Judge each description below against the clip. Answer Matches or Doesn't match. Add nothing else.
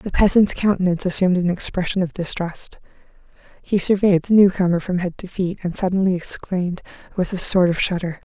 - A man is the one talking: Doesn't match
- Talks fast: Doesn't match